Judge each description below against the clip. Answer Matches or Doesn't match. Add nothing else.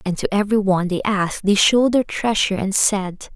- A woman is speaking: Matches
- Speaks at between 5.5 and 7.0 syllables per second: Matches